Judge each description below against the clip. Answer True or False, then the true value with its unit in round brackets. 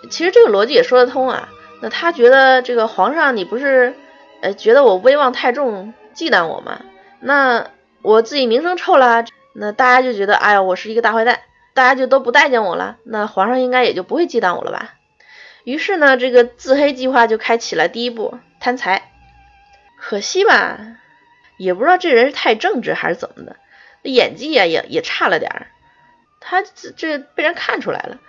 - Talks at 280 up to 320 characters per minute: True (285 characters per minute)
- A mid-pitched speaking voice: False (255 Hz)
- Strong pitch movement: True (5.9 semitones)